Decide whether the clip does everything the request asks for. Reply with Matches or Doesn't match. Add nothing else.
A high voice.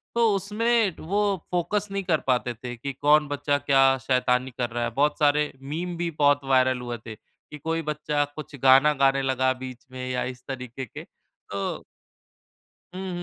Doesn't match